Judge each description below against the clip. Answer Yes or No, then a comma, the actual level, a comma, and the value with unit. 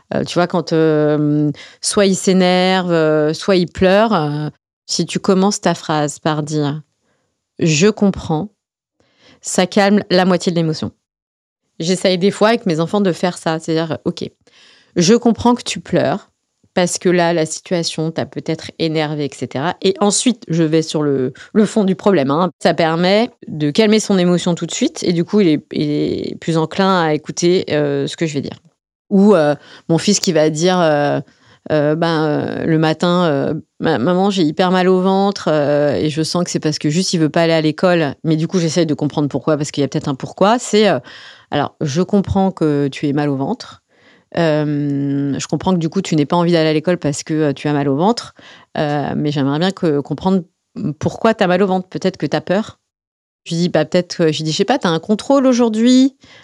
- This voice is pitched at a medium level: Yes, medium, 170 Hz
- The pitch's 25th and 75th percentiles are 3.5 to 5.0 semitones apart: Yes, average, 3.8 semitones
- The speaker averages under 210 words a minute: No, average, 215 wpm